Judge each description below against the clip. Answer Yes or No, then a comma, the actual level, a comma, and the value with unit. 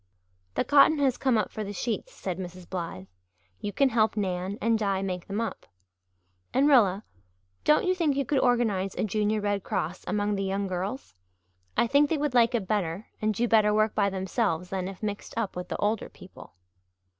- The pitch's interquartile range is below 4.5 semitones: Yes, average, 3.8 semitones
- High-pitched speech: Yes, high, 210 Hz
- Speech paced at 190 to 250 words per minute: Yes, average, 200 wpm